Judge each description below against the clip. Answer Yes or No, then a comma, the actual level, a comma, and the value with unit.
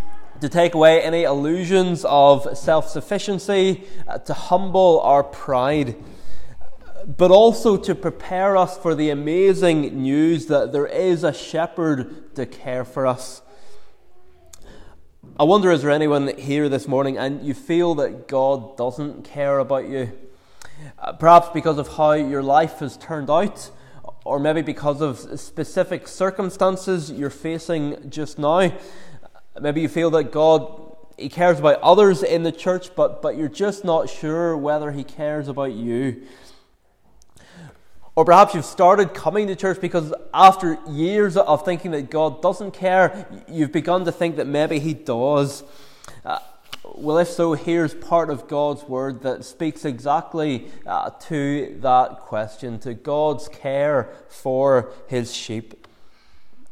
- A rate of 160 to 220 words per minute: No, average, 145 wpm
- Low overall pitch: No, medium, 155 Hz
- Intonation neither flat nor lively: Yes, average, 3.8 semitones